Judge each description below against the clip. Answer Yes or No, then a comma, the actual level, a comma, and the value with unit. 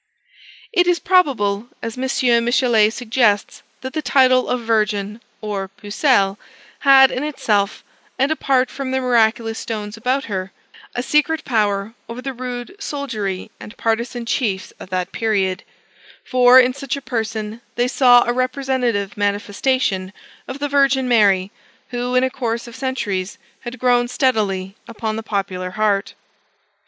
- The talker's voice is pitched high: Yes, high, 235 Hz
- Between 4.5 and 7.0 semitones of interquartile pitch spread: No, average, 3.9 semitones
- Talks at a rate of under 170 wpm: Yes, average, 145 wpm